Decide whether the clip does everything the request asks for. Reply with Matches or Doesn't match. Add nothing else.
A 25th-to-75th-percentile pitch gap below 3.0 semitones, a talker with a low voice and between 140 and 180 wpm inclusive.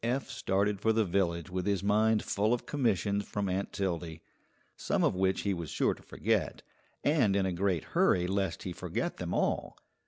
Doesn't match